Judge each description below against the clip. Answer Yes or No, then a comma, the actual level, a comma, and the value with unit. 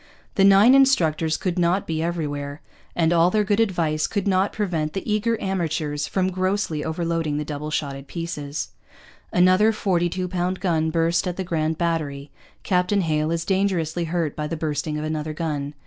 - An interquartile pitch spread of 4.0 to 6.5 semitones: No, average, 3.3 semitones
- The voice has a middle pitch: Yes, medium, 170 Hz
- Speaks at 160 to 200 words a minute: Yes, average, 170 wpm